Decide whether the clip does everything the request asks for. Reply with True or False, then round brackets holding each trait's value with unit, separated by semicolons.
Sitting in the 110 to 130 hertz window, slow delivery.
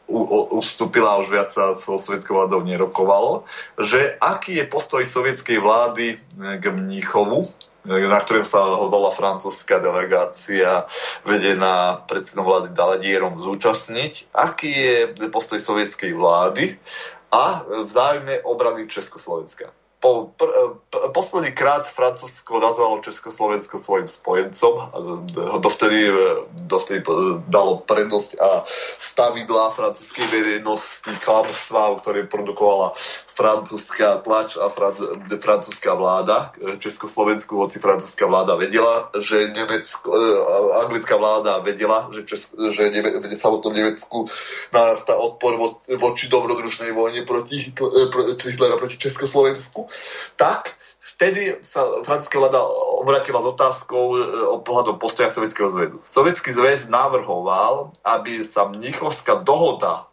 False (115 Hz; 120 wpm)